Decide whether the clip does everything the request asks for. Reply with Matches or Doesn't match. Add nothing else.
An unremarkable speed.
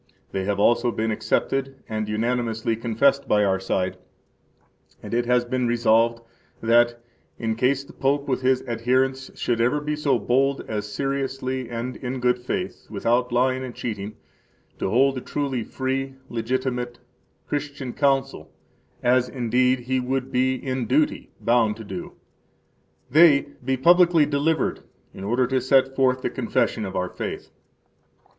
Matches